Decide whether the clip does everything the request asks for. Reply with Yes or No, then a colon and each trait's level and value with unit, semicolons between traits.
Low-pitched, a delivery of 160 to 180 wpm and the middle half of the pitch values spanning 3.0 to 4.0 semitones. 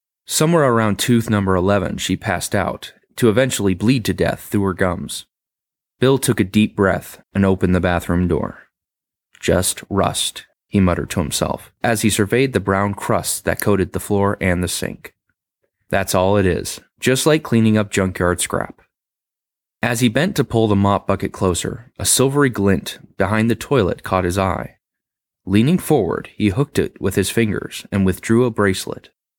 Yes: low, 100 Hz; average, 175 wpm; average, 3.7 semitones